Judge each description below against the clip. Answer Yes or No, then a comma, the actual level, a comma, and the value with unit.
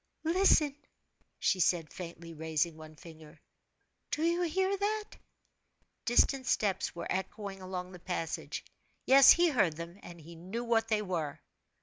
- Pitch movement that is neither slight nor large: No, wide, 8.5 semitones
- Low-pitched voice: No, high, 190 Hz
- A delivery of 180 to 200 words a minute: No, slow, 135 wpm